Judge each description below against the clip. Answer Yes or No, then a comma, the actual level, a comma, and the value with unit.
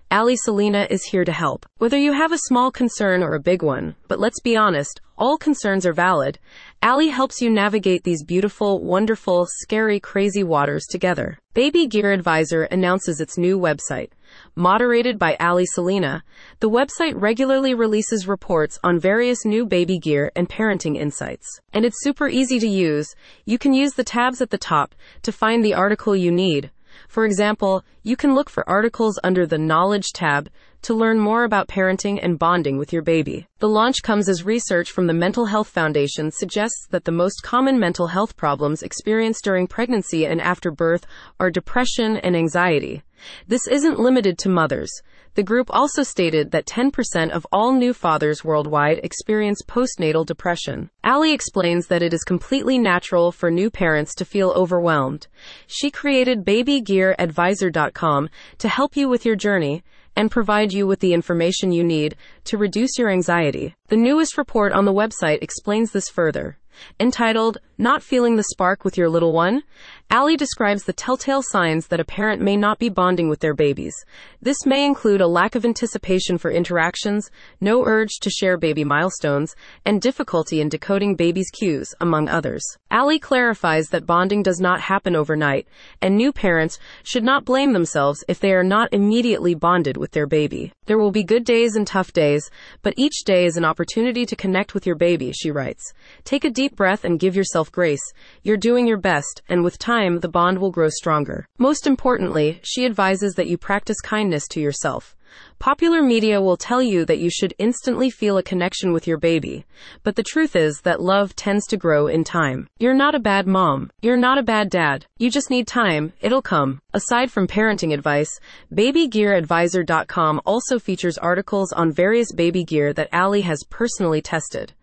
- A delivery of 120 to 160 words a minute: No, average, 180 wpm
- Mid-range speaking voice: No, high, 195 Hz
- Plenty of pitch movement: No, average, 5.0 semitones